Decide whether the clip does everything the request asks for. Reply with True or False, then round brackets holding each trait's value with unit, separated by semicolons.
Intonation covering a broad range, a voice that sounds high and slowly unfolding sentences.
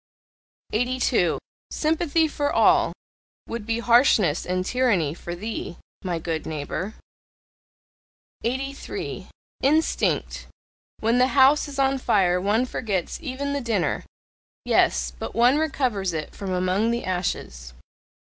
True (6.7 semitones; 230 Hz; 120 wpm)